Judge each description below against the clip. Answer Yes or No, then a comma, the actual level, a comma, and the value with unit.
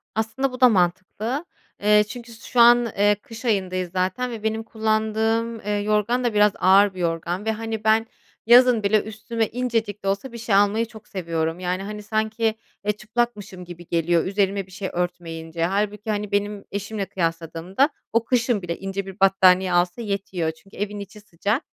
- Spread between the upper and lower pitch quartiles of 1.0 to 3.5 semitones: Yes, average, 3.0 semitones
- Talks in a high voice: Yes, high, 205 Hz